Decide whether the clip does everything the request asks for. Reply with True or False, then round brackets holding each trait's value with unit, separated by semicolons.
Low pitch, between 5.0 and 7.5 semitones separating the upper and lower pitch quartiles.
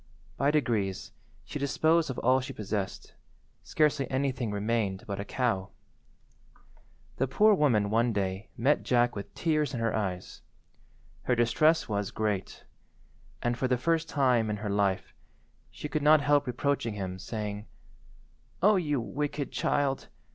True (120 Hz; 5.6 semitones)